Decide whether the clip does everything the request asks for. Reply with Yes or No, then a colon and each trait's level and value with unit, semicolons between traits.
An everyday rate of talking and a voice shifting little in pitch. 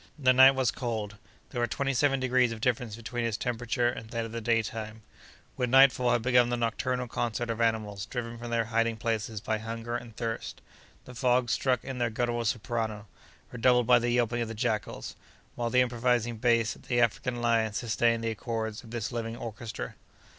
Yes: average, 195 wpm; narrow, 1.4 semitones